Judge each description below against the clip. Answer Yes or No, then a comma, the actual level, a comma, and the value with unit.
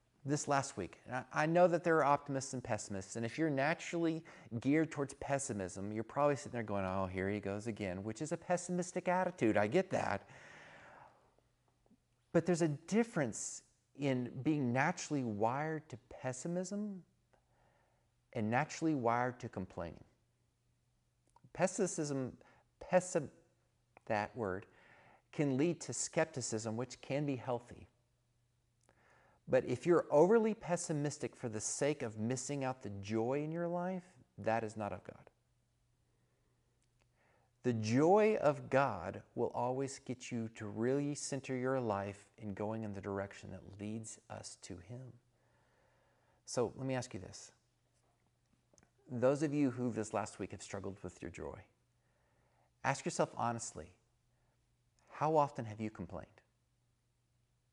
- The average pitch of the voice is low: Yes, low, 125 Hz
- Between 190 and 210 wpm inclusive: No, slow, 135 wpm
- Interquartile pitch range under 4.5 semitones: No, average, 4.8 semitones